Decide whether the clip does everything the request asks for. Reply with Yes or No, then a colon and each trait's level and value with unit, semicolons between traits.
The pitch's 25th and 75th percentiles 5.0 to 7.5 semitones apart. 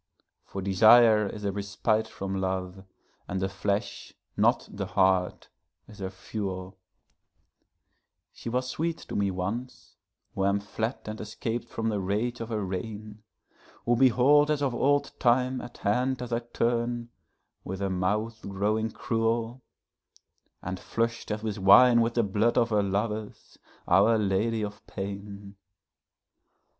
No: average, 3.2 semitones